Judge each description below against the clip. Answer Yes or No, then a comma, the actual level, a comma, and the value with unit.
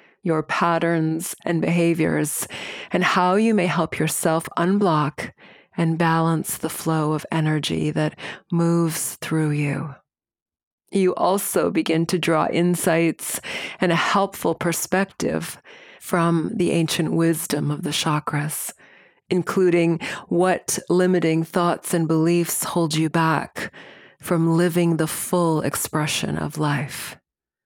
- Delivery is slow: Yes, slow, 115 wpm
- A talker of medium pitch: Yes, medium, 165 Hz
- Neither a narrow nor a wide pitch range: No, narrow, 1.9 semitones